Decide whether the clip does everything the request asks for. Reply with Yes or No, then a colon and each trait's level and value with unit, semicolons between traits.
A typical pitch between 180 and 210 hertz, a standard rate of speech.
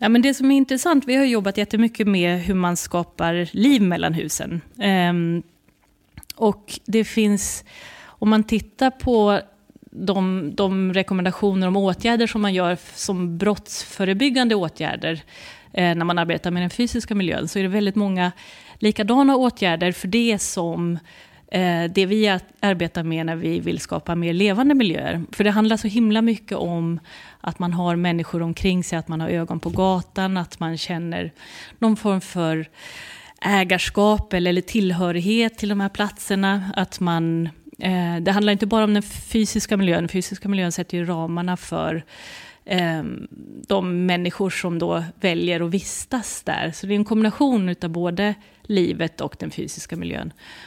Yes: high, 190 Hz; average, 155 wpm